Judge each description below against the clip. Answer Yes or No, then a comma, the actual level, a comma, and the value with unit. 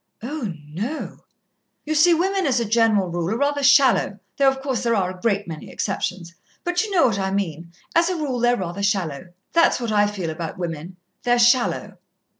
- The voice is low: No, high, 225 Hz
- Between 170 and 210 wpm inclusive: Yes, average, 200 wpm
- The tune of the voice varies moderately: No, wide, 7.1 semitones